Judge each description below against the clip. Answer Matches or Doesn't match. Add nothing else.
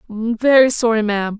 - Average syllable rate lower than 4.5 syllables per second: Doesn't match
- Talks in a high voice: Matches